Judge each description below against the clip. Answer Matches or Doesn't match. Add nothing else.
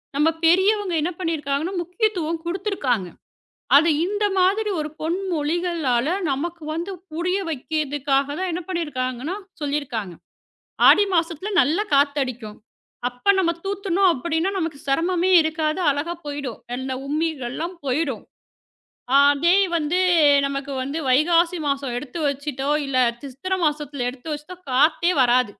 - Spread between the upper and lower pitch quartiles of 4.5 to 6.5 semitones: Doesn't match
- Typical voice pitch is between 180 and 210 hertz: Doesn't match